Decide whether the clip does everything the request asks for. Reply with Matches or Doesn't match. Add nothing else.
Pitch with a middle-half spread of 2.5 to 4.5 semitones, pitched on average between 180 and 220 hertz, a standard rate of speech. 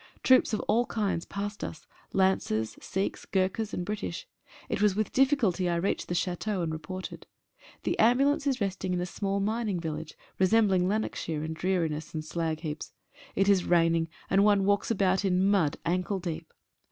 Matches